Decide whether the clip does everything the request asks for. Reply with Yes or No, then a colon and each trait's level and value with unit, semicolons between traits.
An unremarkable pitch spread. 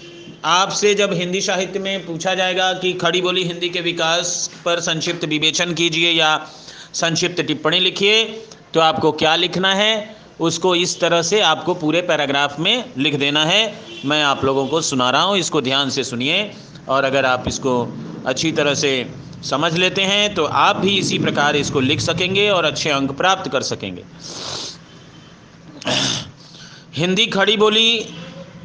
Yes: average, 3.8 semitones